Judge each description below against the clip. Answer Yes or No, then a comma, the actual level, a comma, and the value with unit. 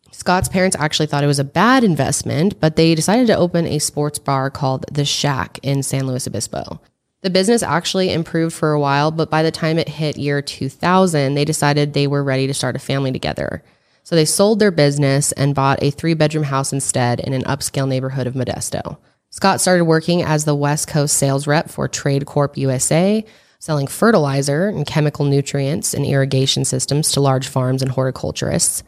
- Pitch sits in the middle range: Yes, medium, 145 Hz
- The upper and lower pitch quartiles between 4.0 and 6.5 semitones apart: No, average, 3.0 semitones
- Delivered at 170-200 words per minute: Yes, average, 195 wpm